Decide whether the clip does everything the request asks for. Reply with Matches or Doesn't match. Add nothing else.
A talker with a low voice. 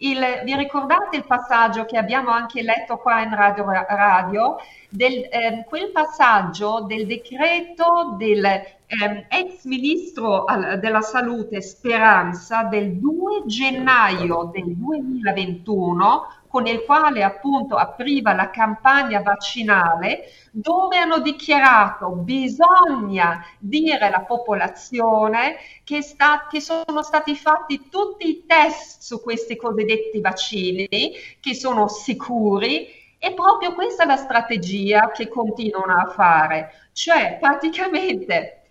Doesn't match